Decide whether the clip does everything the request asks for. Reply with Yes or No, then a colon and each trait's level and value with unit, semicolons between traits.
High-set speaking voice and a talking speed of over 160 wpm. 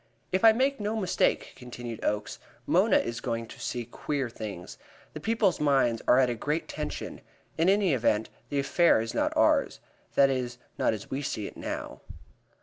No: low, 130 Hz; average, 180 wpm